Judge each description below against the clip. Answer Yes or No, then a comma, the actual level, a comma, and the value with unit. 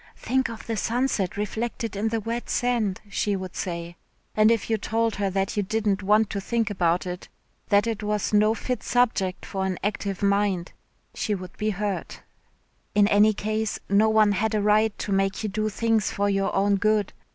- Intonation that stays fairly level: Yes, narrow, 2.0 semitones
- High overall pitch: Yes, high, 210 Hz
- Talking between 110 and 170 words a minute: No, average, 195 wpm